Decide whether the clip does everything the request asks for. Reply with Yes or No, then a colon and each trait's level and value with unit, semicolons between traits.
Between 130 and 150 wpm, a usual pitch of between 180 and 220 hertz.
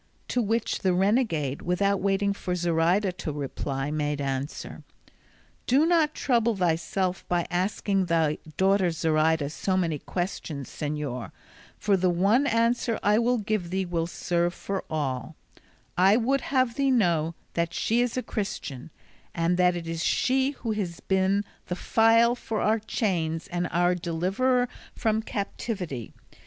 Yes: average, 145 wpm; medium, 185 Hz